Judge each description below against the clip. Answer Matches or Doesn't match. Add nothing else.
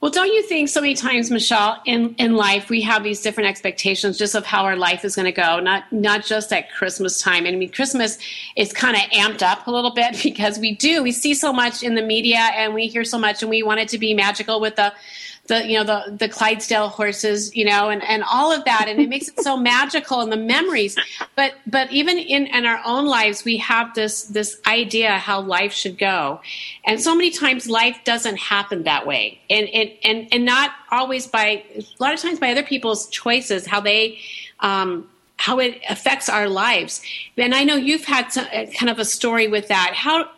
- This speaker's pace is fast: Matches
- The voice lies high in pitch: Matches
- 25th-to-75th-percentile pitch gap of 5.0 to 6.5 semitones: Doesn't match